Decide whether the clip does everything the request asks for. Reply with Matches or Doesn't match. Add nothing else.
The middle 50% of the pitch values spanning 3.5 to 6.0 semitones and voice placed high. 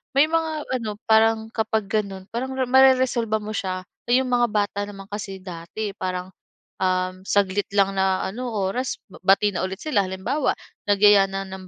Matches